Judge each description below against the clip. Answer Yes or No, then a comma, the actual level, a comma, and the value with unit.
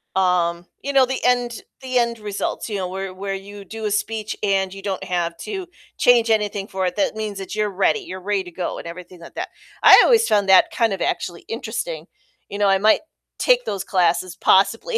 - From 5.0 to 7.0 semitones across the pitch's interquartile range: No, average, 3.3 semitones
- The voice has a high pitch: Yes, high, 200 Hz